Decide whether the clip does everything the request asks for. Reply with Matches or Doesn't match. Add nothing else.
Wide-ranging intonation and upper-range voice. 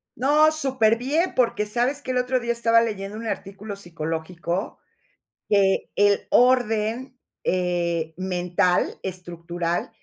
Matches